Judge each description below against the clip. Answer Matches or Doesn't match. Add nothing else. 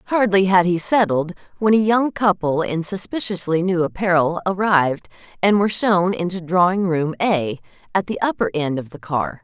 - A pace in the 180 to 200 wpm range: Doesn't match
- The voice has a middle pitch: Matches